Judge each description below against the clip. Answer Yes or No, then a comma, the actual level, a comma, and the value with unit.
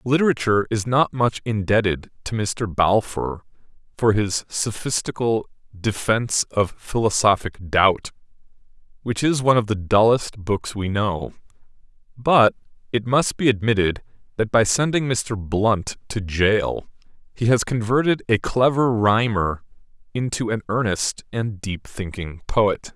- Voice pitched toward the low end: Yes, low, 110 Hz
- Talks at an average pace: No, slow, 130 wpm